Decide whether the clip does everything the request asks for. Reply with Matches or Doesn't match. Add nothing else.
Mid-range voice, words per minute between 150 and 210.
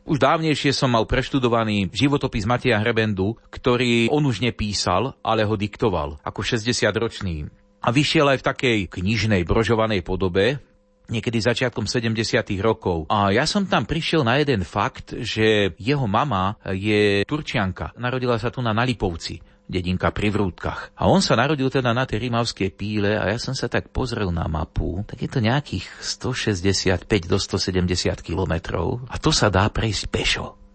Doesn't match